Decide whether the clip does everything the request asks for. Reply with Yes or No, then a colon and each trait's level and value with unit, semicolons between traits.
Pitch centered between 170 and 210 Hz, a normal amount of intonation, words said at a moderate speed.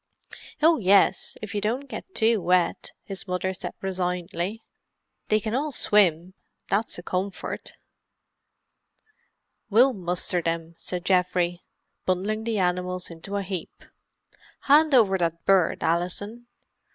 No: high, 190 Hz; average, 3.3 semitones; slow, 125 wpm